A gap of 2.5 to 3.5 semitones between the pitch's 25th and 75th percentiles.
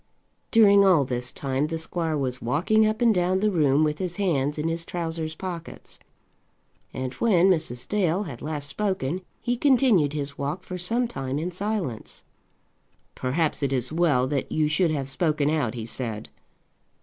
No: average, 5.1 semitones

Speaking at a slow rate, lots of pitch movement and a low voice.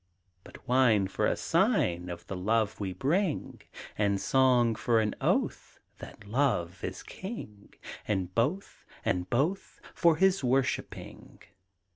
Yes: slow, 130 wpm; wide, 5.9 semitones; low, 115 Hz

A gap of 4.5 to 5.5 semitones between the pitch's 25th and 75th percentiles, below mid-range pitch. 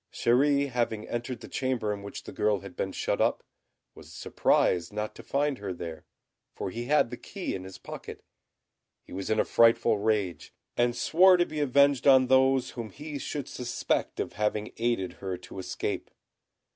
Yes: average, 4.8 semitones; low, 120 Hz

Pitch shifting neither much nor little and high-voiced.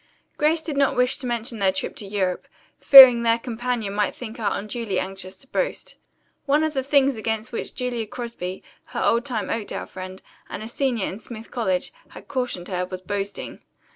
Yes: average, 4.2 semitones; high, 230 Hz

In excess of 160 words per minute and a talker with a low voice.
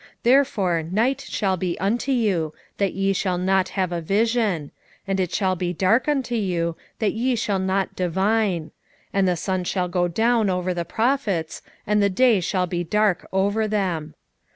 No: average, 175 wpm; high, 190 Hz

